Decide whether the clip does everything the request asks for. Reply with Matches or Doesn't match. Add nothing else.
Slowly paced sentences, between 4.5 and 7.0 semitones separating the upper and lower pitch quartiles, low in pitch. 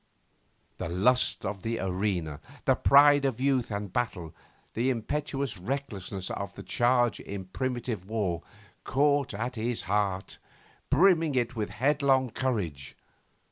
Matches